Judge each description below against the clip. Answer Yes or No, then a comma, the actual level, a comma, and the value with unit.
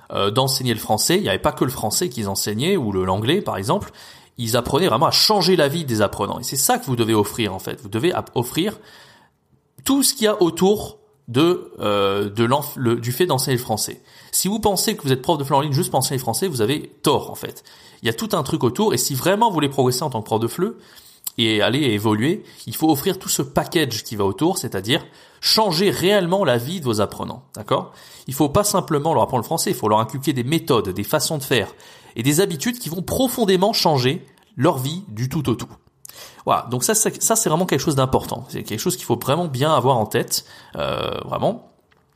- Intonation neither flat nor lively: No, wide, 7.9 semitones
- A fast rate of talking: Yes, fast, 240 wpm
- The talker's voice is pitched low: No, medium, 145 Hz